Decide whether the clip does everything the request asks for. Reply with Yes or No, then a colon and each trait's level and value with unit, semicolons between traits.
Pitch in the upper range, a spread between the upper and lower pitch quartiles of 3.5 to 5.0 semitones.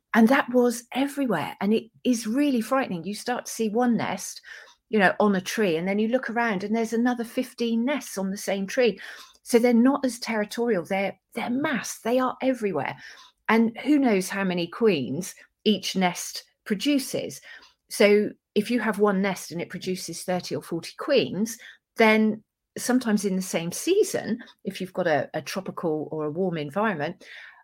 Yes: high, 220 Hz; average, 4.2 semitones